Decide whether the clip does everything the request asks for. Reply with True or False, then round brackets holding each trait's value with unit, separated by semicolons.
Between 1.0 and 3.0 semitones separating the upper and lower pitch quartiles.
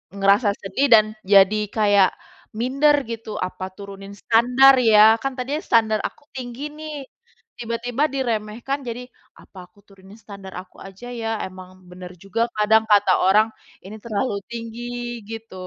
False (3.6 semitones)